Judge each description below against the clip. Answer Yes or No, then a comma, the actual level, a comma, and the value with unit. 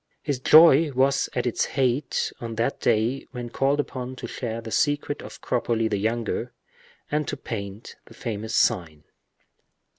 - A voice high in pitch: No, low, 125 Hz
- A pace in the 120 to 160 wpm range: Yes, average, 155 wpm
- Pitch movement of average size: Yes, average, 3.5 semitones